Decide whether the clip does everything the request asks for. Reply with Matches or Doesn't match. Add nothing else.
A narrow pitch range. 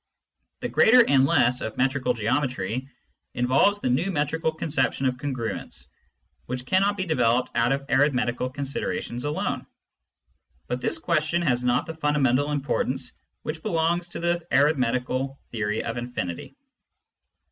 Doesn't match